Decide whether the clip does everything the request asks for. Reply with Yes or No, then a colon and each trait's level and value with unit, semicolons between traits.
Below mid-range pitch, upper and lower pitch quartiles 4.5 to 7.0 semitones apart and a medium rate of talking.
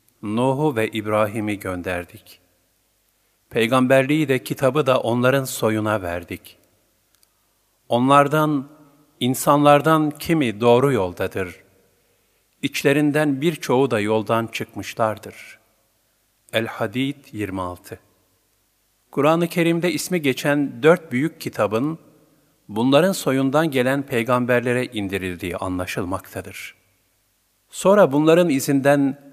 No: low, 120 Hz; wide, 5.6 semitones; slow, 80 wpm